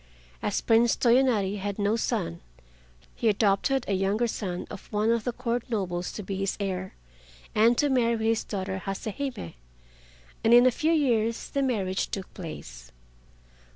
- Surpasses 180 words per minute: No, average, 160 wpm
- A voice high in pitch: Yes, high, 215 Hz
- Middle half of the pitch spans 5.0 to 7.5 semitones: No, average, 3.7 semitones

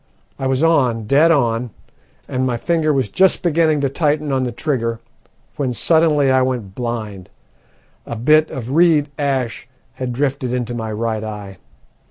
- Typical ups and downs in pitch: Yes, average, 4.2 semitones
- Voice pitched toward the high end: No, low, 130 Hz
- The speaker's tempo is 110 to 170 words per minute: Yes, average, 160 wpm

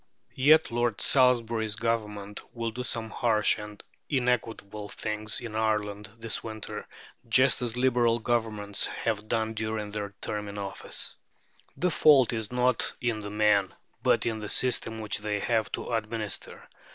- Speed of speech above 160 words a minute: No, average, 150 wpm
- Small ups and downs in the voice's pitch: Yes, narrow, 2.2 semitones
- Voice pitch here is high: No, low, 110 Hz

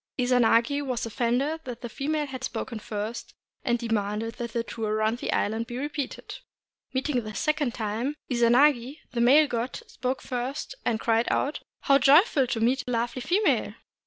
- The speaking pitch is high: Yes, high, 245 Hz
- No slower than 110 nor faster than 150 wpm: No, average, 170 wpm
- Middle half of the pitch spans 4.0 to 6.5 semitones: No, average, 3.2 semitones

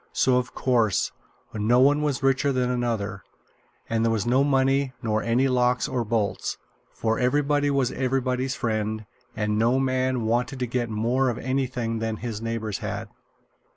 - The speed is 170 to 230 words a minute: No, average, 160 wpm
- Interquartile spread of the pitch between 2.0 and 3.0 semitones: Yes, average, 2.7 semitones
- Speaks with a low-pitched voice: Yes, low, 125 Hz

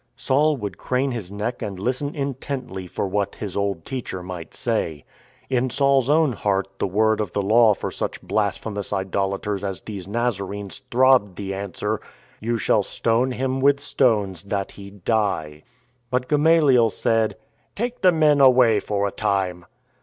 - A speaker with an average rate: Yes, average, 165 wpm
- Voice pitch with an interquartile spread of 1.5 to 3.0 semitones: No, average, 4.7 semitones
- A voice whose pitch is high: No, low, 110 Hz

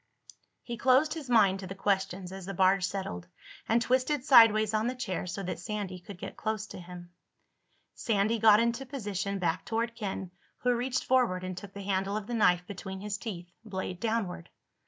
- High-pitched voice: Yes, high, 200 Hz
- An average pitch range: Yes, average, 3.7 semitones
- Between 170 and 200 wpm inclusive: Yes, average, 190 wpm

